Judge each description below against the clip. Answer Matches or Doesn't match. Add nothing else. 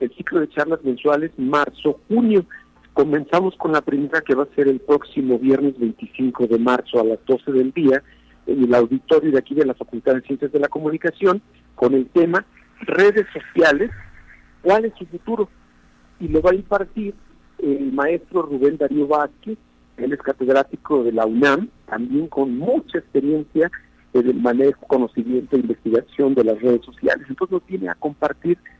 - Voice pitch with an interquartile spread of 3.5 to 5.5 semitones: Matches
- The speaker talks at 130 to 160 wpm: Doesn't match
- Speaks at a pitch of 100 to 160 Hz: Matches